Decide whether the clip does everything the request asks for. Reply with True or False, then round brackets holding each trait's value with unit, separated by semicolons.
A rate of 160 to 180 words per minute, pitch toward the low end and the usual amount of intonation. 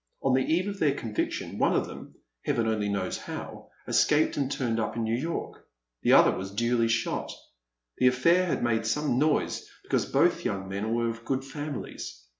False (190 wpm; 120 Hz; 4.3 semitones)